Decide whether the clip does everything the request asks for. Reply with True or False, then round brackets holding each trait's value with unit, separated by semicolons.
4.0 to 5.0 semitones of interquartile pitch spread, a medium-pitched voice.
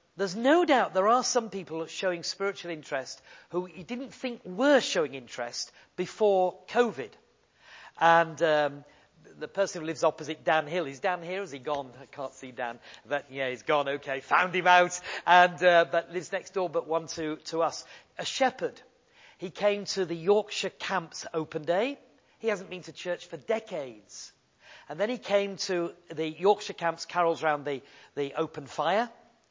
True (4.3 semitones; 175 Hz)